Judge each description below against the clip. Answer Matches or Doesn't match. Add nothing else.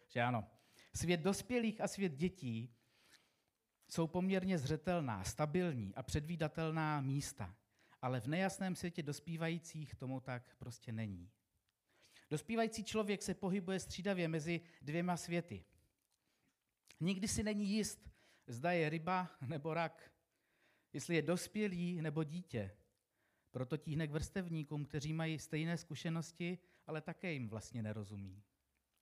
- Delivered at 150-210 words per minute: Doesn't match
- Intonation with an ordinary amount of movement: Doesn't match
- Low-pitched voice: Doesn't match